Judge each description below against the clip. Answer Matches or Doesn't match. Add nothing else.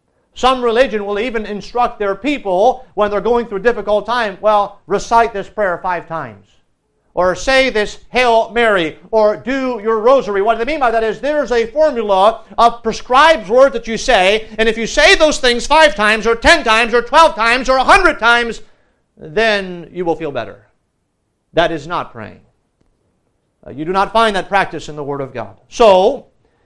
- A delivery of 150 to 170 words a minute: Doesn't match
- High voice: Matches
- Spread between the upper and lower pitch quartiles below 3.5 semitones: Doesn't match